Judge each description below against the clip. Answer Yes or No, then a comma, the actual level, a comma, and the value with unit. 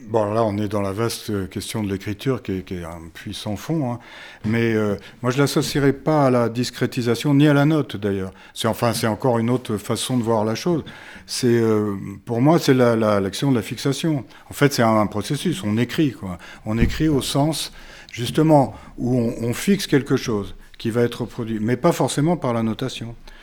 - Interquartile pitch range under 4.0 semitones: No, average, 4.5 semitones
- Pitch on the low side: Yes, low, 120 Hz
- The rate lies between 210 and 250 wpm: Yes, fast, 220 wpm